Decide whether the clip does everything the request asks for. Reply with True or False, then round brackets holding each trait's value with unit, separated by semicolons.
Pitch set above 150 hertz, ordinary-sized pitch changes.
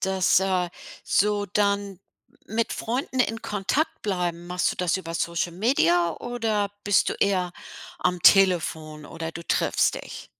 True (190 Hz; 3.0 semitones)